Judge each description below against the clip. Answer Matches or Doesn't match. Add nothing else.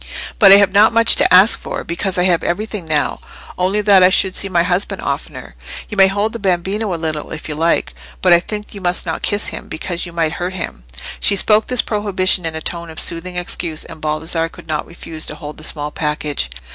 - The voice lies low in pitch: Doesn't match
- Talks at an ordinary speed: Doesn't match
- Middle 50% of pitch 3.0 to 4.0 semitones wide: Matches